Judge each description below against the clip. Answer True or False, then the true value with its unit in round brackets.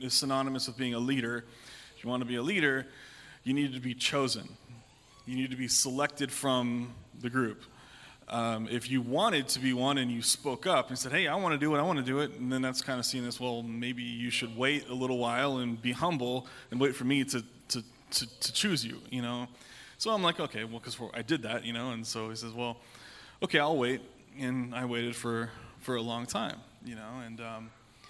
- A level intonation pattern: True (1.8 semitones)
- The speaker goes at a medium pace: False (235 wpm)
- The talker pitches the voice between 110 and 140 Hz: True (125 Hz)